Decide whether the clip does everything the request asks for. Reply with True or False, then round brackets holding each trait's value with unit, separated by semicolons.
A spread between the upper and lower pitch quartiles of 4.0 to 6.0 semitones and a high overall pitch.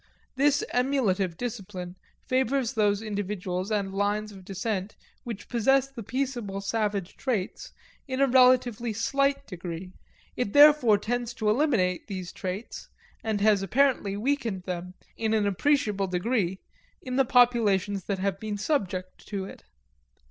True (4.6 semitones; 210 Hz)